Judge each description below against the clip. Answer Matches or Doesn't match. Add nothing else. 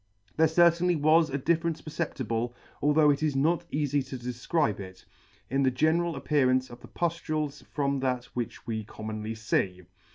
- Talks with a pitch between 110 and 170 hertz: Matches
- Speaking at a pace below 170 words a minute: Matches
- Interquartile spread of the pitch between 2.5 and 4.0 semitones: Doesn't match